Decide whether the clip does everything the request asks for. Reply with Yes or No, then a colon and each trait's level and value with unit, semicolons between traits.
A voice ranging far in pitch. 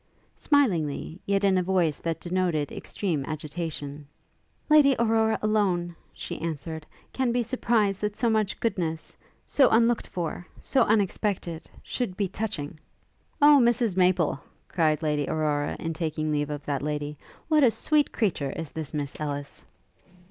Yes: wide, 6.1 semitones